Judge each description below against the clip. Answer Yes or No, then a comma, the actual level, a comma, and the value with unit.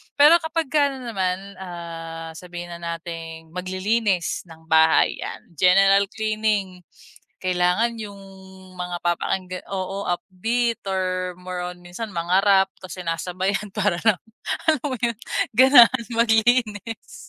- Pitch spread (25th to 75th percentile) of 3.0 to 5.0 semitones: Yes, average, 3.9 semitones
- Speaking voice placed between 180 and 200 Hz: Yes, high, 190 Hz